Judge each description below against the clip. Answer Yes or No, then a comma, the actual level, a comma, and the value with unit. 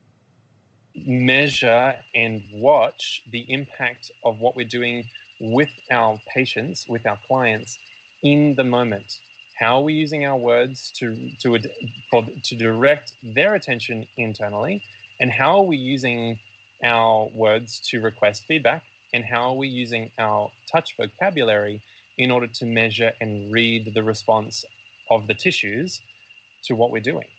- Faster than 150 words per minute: No, average, 140 wpm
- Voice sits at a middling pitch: No, low, 120 Hz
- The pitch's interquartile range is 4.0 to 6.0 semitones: No, narrow, 2.6 semitones